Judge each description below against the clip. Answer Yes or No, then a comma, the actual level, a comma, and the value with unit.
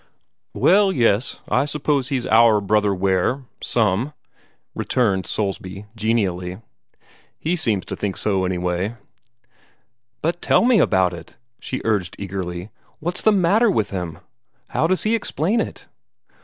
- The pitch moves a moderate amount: No, wide, 8.1 semitones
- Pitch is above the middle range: No, low, 110 Hz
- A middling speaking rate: No, slow, 130 wpm